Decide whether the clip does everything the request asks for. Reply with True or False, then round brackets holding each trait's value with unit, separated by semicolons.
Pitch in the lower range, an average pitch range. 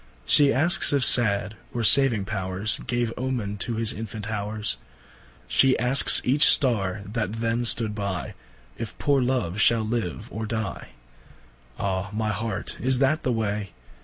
True (110 Hz; 3.4 semitones)